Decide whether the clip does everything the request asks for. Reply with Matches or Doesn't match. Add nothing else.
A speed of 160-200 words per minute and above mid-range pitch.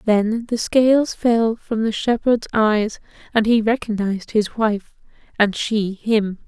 Doesn't match